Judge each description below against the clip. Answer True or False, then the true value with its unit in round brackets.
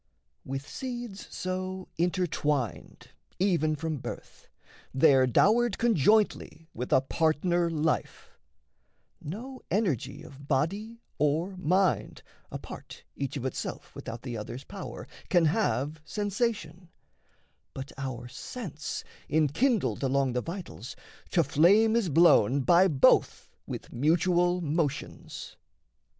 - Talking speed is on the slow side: True (110 wpm)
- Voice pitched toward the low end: False (165 Hz)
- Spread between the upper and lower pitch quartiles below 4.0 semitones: False (5.4 semitones)